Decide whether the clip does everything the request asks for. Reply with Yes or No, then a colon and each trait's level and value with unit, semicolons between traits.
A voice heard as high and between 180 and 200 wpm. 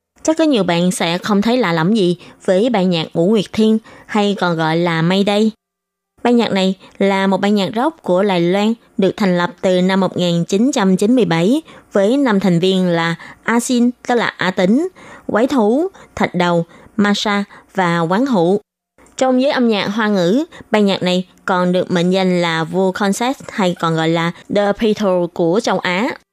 Yes: high, 195 Hz; average, 185 wpm